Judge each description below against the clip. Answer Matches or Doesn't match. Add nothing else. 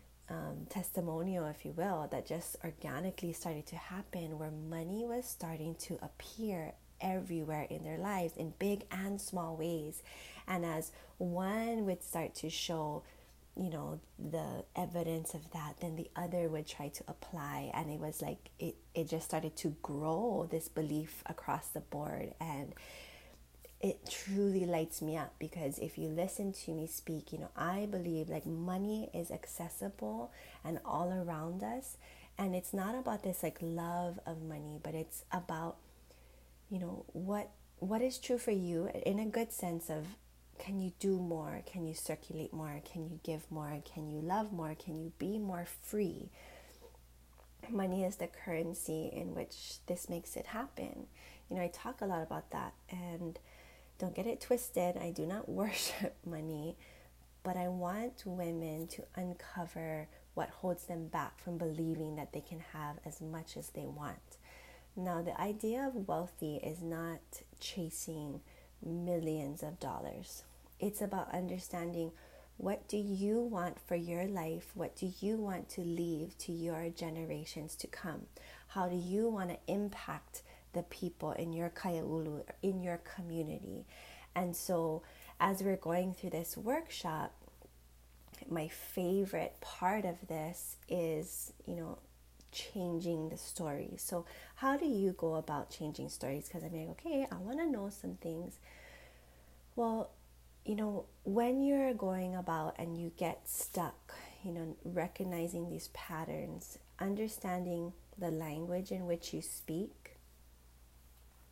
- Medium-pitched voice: Matches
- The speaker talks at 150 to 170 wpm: Matches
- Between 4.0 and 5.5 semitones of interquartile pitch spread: Doesn't match